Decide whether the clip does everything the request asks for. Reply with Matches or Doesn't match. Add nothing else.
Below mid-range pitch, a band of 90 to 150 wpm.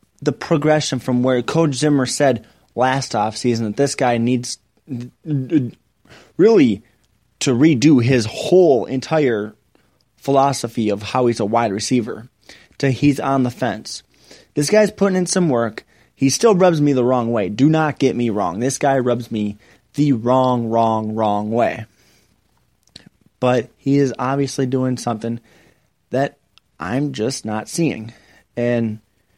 Matches